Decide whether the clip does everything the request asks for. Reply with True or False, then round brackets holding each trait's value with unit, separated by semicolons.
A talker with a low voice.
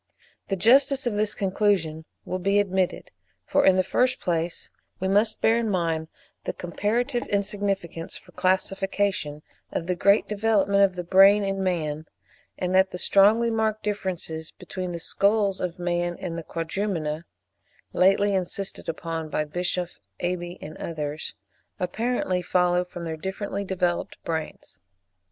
False (185 Hz)